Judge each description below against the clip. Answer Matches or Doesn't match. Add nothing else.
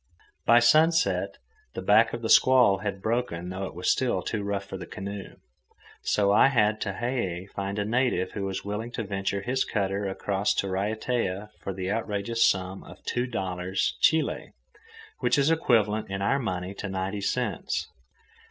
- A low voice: Matches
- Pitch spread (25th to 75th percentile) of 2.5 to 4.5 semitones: Matches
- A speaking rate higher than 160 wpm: Matches